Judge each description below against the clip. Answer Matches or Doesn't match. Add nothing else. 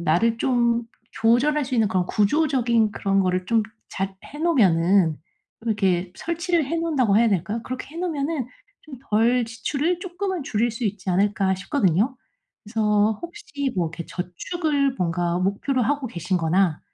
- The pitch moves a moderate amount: Doesn't match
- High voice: Matches